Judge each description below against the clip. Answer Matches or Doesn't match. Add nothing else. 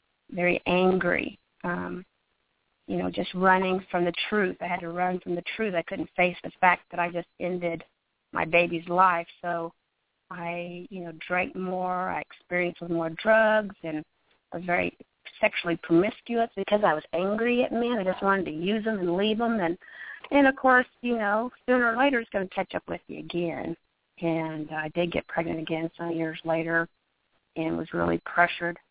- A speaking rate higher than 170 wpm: Matches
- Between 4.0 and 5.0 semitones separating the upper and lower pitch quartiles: Doesn't match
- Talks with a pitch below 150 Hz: Doesn't match